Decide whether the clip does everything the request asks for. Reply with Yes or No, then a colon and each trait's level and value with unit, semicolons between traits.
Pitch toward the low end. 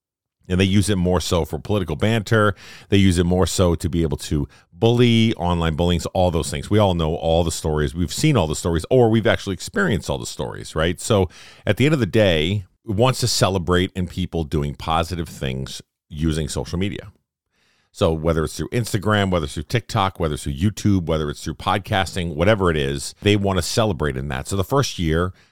Yes: very low, 90 Hz